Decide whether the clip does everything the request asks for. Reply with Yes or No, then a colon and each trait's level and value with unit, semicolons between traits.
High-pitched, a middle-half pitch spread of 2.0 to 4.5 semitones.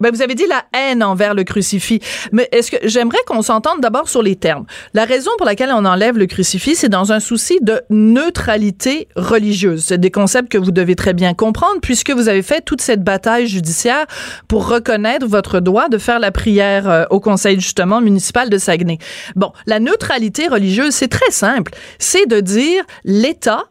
Yes: high, 220 Hz; average, 4.0 semitones